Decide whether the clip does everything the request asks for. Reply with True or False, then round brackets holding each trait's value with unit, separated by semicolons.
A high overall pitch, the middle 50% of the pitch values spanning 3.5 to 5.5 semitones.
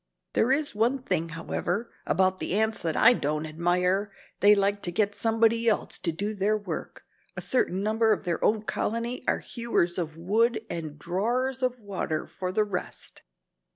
True (205 Hz; 4.4 semitones)